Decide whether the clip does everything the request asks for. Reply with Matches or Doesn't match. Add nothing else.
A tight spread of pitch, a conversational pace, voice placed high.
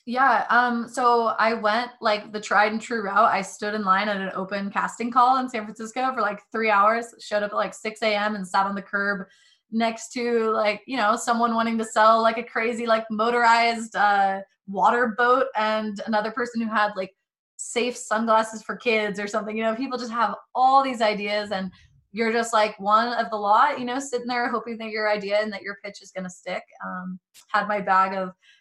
Doesn't match